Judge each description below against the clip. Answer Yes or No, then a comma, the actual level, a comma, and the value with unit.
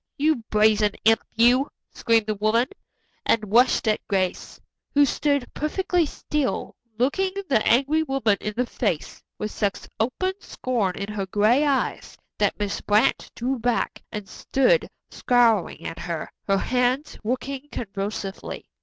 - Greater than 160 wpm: No, average, 140 wpm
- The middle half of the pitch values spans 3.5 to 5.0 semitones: Yes, average, 4.4 semitones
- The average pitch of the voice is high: Yes, high, 235 Hz